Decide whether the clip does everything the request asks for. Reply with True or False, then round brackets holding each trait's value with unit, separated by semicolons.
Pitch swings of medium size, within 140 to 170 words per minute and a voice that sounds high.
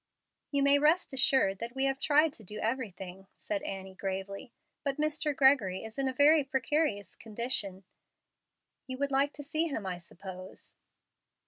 False (6.5 semitones; 160 wpm; 260 Hz)